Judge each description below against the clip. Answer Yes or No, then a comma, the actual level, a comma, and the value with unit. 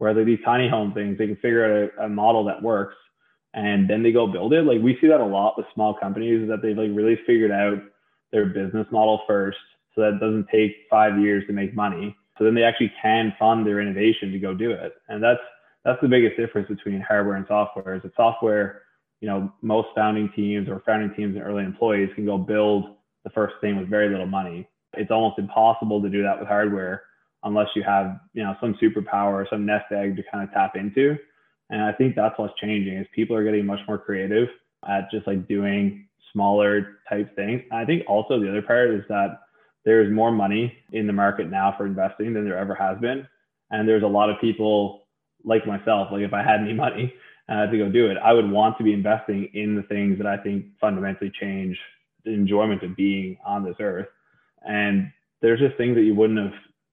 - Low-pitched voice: Yes, low, 105 Hz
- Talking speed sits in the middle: No, fast, 225 wpm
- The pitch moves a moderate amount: No, narrow, 1.6 semitones